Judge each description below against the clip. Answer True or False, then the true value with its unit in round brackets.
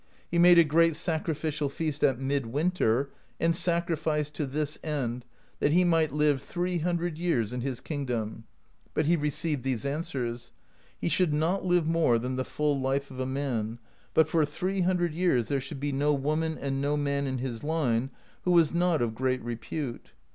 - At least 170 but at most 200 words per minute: True (185 wpm)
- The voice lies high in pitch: False (150 Hz)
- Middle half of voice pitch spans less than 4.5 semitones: True (3.9 semitones)